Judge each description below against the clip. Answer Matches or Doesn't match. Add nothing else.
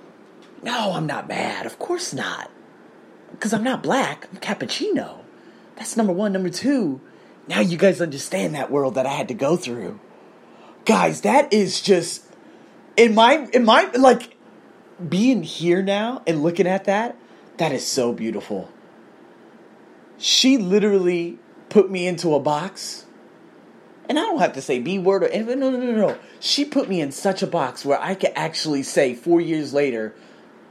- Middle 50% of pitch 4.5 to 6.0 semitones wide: Matches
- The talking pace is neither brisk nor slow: Matches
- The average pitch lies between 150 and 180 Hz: Doesn't match